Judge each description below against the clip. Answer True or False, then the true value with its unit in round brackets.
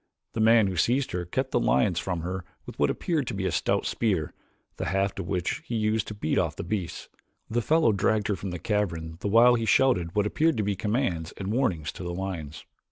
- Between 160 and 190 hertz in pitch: False (100 Hz)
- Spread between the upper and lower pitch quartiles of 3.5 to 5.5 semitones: True (4.4 semitones)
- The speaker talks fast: True (230 wpm)